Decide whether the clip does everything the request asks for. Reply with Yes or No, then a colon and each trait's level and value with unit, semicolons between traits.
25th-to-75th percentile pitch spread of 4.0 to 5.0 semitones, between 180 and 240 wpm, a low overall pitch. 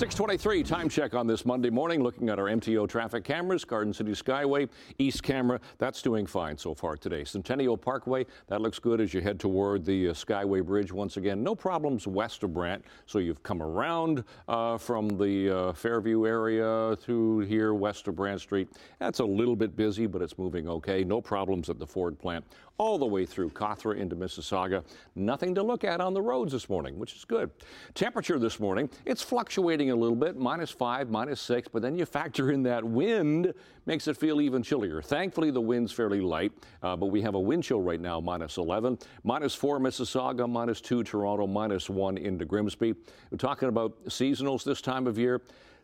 Yes: average, 4.5 semitones; average, 200 wpm; low, 115 Hz